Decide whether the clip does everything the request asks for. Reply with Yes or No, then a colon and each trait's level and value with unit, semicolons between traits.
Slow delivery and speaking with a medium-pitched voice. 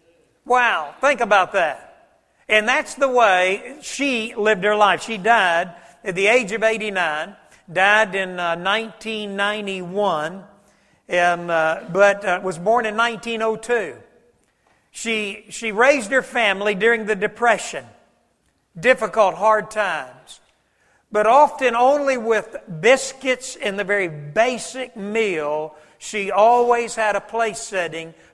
No: slow, 125 wpm; high, 215 Hz